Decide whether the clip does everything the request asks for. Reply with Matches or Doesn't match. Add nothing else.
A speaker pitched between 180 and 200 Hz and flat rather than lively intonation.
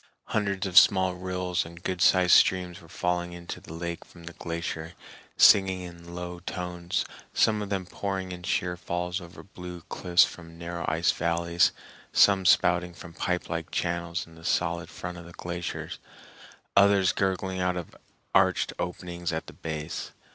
Doesn't match